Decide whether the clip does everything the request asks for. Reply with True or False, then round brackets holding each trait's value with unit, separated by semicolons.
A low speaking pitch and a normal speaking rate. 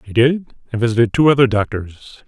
True (120 Hz; 185 wpm)